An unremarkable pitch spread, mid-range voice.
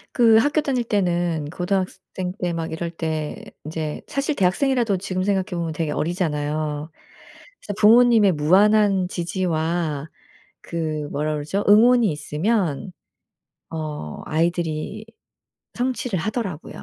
Yes: average, 5.0 semitones; medium, 175 Hz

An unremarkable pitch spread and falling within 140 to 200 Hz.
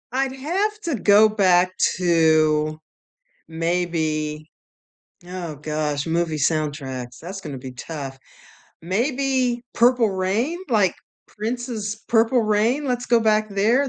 No: wide, 7.3 semitones; high, 190 Hz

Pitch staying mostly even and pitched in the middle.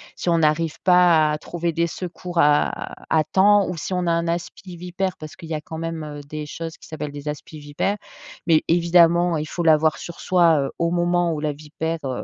Yes: narrow, 2.2 semitones; medium, 165 Hz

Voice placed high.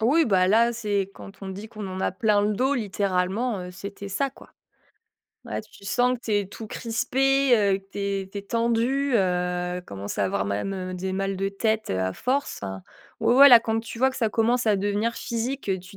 Yes: high, 205 Hz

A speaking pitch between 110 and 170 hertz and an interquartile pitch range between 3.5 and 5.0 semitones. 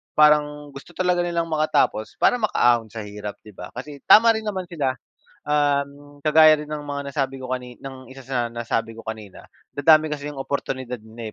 Yes: medium, 140 Hz; average, 4.1 semitones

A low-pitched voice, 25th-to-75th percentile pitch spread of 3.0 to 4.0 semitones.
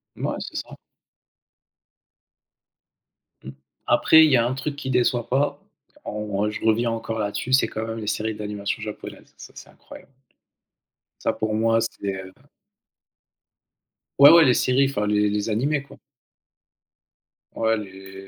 Yes: low, 110 Hz; average, 3.7 semitones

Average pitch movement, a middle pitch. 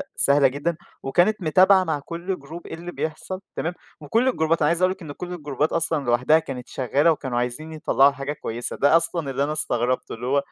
Yes: average, 3.7 semitones; medium, 155 Hz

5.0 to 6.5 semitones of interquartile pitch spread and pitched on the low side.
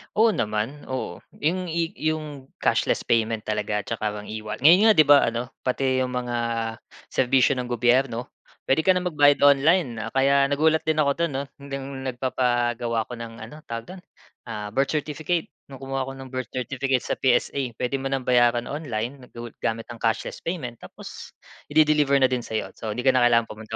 No: average, 3.5 semitones; low, 130 Hz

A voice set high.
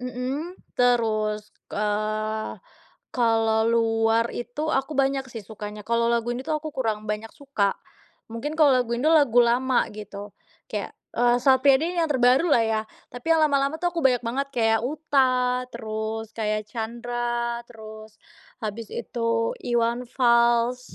Yes: high, 235 Hz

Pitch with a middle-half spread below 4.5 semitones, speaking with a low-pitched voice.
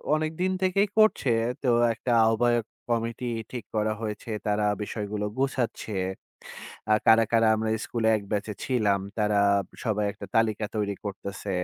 Yes: narrow, 2.6 semitones; low, 110 Hz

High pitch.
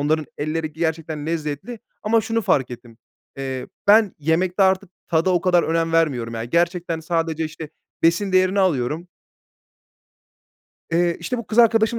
No: medium, 165 Hz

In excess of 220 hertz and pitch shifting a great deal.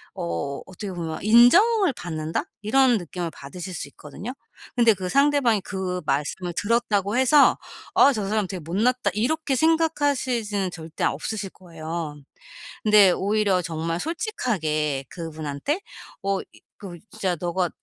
No: high, 195 Hz; wide, 6.4 semitones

